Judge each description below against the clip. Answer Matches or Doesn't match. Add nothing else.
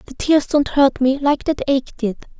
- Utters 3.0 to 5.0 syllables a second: Matches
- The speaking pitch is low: Doesn't match